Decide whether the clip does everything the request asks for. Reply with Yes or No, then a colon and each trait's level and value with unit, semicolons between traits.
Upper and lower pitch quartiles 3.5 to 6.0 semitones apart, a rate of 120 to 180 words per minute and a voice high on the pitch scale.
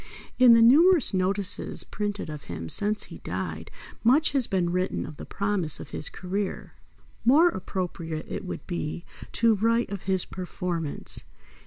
Yes: average, 4.7 semitones; average, 155 wpm; high, 195 Hz